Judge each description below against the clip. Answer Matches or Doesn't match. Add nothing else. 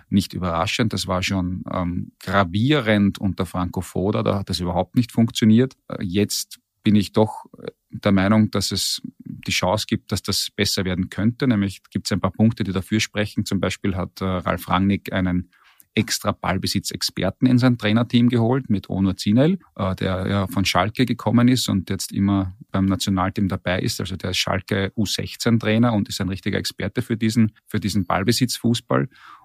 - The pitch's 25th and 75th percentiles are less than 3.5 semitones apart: Matches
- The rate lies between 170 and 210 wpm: Matches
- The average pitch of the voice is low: Matches